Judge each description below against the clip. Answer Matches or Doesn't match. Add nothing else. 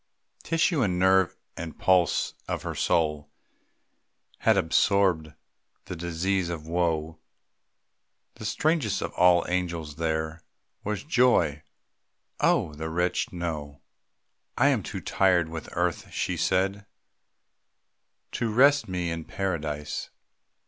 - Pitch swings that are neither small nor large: Matches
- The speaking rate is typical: Doesn't match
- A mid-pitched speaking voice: Doesn't match